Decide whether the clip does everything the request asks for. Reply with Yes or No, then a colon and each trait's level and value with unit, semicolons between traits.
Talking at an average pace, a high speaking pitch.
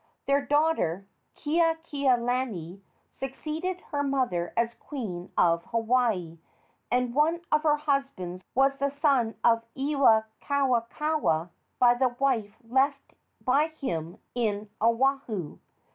No: slow, 105 wpm; very high, 255 Hz